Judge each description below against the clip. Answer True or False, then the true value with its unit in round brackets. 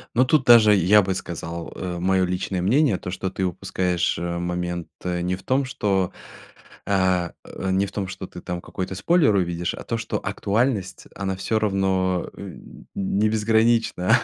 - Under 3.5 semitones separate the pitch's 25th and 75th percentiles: True (2.9 semitones)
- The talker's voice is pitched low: True (95 Hz)